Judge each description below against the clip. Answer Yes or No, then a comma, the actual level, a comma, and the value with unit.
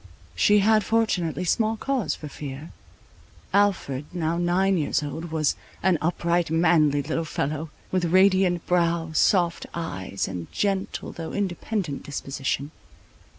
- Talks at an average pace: No, slow, 125 wpm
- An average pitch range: Yes, average, 3.8 semitones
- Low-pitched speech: No, medium, 170 Hz